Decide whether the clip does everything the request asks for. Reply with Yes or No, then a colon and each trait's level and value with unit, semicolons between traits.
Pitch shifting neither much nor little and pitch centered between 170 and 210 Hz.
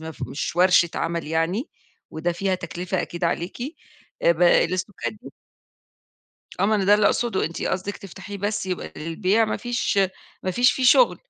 Yes: average, 3.3 semitones; medium, 185 Hz